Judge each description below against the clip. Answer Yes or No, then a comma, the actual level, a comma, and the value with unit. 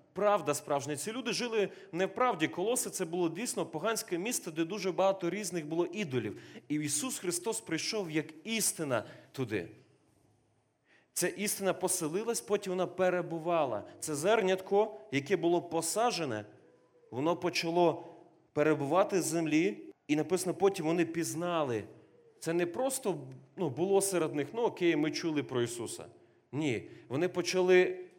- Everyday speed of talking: Yes, average, 135 wpm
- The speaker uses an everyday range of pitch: Yes, average, 3.6 semitones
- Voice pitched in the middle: Yes, medium, 175 Hz